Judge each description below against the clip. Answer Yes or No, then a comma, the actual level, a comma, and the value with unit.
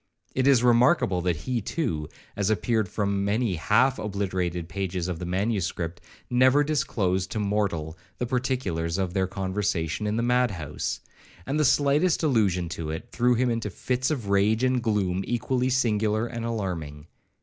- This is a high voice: No, low, 105 Hz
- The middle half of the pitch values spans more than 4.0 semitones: Yes, average, 5.2 semitones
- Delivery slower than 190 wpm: Yes, average, 160 wpm